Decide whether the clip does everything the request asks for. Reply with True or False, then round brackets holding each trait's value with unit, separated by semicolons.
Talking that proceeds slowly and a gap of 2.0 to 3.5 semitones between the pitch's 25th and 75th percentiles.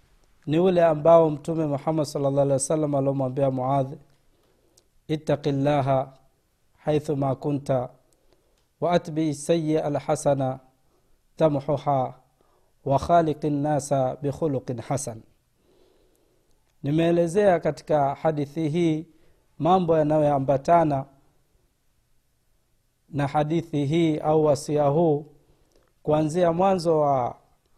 True (80 wpm; 2.6 semitones)